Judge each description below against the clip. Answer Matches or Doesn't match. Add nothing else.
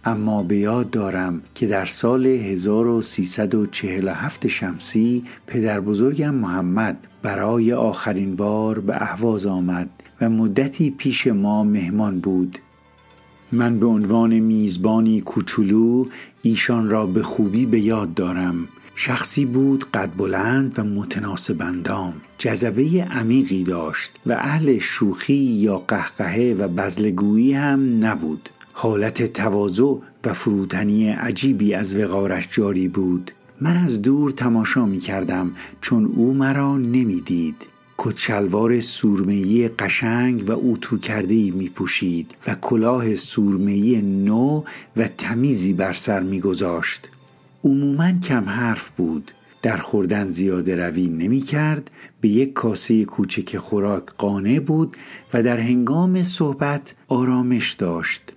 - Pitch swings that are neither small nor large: Matches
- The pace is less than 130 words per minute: Matches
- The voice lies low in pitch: Matches